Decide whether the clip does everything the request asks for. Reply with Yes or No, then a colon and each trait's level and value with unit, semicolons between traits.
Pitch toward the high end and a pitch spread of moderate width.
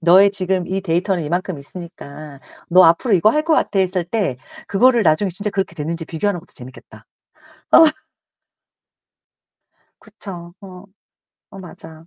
No: medium, 180 Hz; average, 3.0 semitones